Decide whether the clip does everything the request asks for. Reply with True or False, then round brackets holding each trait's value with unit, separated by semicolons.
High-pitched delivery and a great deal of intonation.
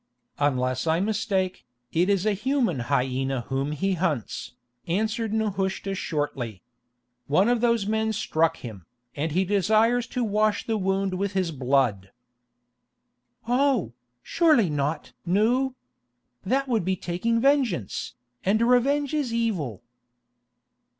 True (195 Hz; 7.4 semitones)